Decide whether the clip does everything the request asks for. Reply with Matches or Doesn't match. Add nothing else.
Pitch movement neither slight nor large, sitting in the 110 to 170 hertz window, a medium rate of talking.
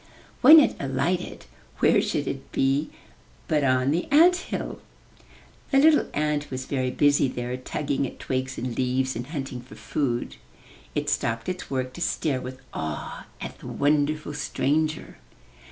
Matches